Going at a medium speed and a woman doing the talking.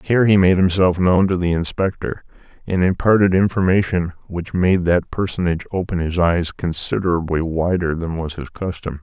No: average, 160 wpm; male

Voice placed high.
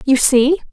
Yes: very high, 275 Hz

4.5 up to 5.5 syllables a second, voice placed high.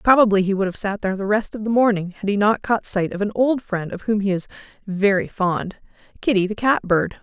No: 5.8 syllables/s; high, 205 Hz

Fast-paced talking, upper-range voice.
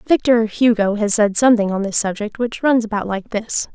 Yes: fast, 210 wpm; high, 220 Hz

